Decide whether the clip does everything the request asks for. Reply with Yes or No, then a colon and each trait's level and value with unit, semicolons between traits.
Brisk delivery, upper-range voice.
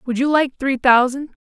Yes: fast, 210 wpm; very high, 265 Hz